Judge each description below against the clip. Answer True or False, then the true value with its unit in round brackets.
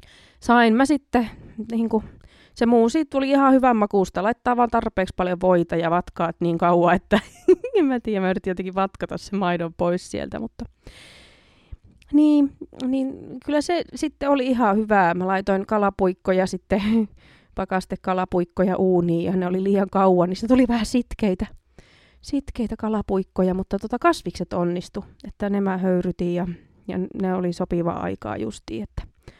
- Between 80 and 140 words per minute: False (155 wpm)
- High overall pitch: True (195 Hz)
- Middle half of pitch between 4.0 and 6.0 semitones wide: True (4.8 semitones)